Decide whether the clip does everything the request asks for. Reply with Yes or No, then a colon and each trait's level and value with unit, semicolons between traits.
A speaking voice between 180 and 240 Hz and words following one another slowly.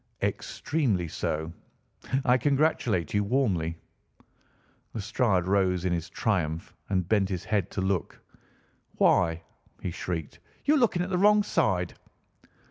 No: very low, 95 Hz; slow, 125 wpm